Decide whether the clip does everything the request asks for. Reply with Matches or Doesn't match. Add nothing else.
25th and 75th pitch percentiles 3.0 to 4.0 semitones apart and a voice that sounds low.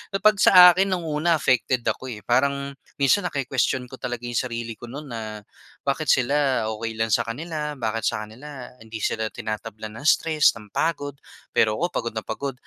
Doesn't match